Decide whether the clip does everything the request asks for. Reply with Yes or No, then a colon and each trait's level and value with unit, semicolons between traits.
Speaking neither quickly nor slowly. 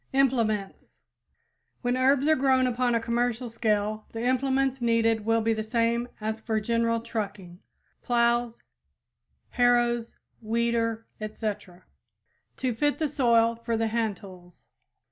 No: slow, 125 wpm